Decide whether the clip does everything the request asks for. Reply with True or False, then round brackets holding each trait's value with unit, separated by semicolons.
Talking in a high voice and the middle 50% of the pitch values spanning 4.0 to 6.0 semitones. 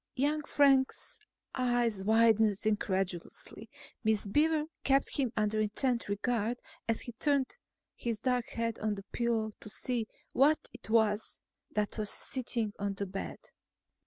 False (225 Hz; 3.3 semitones)